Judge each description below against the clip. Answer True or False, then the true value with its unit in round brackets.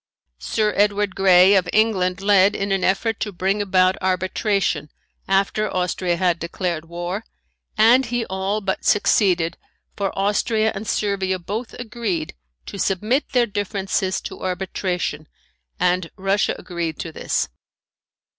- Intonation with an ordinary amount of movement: False (2.3 semitones)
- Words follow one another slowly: True (130 wpm)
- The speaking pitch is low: False (195 Hz)